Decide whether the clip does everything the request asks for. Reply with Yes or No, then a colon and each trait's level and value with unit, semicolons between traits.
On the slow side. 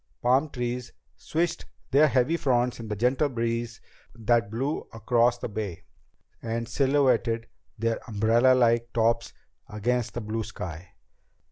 Yes: slow, 125 wpm